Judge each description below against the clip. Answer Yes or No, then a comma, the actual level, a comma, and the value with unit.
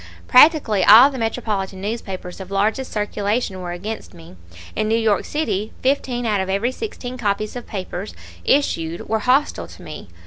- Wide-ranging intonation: No, average, 4.2 semitones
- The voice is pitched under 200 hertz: No, high, 215 Hz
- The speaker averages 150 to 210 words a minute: Yes, average, 165 wpm